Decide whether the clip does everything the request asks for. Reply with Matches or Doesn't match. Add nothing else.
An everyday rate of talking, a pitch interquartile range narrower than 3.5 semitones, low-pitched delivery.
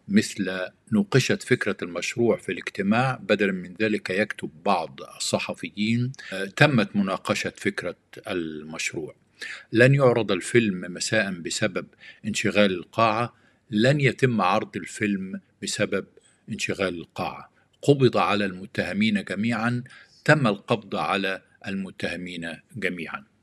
Doesn't match